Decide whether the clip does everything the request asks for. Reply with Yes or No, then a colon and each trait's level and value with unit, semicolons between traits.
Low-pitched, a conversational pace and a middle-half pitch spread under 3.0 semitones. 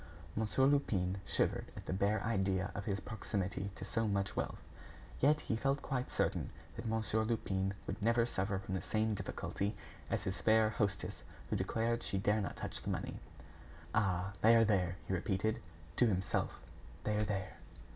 Yes: low, 105 Hz; average, 175 wpm; narrow, 2.6 semitones